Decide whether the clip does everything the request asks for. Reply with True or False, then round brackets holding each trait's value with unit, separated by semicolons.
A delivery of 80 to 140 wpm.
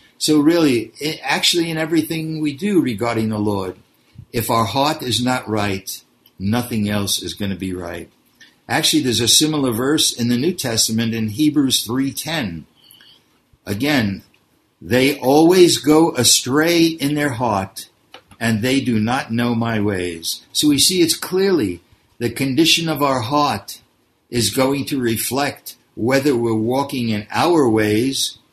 False (150 wpm)